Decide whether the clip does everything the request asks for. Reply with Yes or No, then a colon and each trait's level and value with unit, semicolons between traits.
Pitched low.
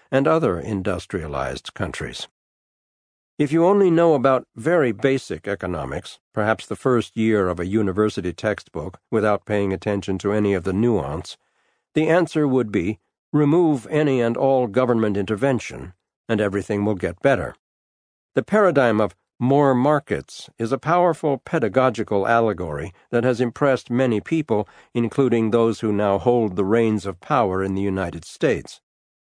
Yes: low, 110 Hz